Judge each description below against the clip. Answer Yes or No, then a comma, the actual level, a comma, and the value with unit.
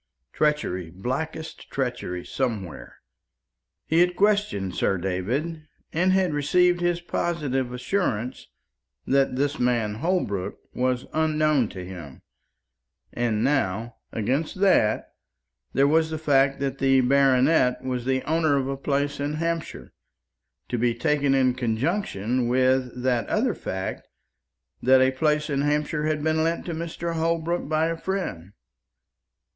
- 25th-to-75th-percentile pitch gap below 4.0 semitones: No, average, 4.6 semitones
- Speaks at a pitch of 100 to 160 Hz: Yes, medium, 140 Hz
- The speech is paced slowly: Yes, slow, 130 wpm